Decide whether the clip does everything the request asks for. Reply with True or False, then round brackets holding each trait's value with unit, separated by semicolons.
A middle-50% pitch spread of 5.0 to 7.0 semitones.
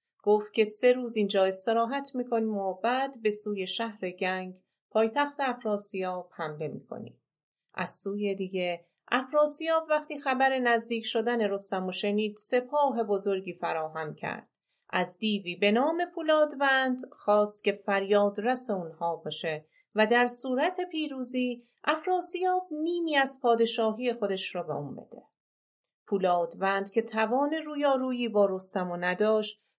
True (5.4 semitones)